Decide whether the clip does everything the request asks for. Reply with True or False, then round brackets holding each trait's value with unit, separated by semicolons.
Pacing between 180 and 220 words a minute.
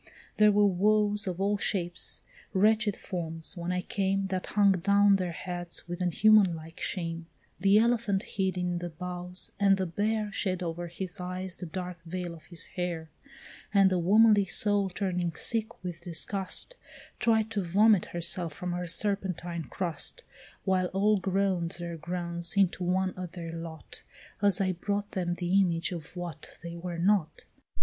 False (165 wpm)